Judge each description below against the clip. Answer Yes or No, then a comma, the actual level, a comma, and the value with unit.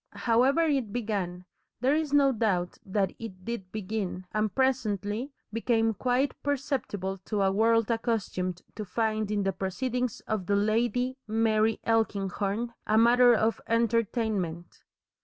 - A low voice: No, high, 220 Hz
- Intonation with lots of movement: No, average, 3.3 semitones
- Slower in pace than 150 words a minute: Yes, slow, 135 wpm